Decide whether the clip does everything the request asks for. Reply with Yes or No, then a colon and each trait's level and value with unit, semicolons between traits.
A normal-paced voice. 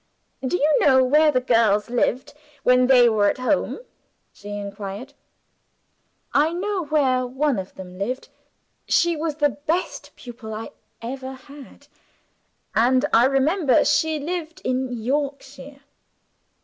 No: slow, 130 wpm